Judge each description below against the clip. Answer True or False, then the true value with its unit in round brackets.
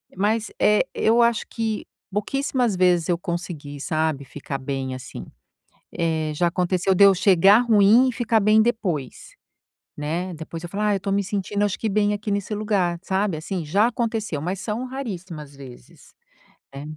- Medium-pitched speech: False (195 Hz)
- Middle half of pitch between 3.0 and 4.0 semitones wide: False (4.5 semitones)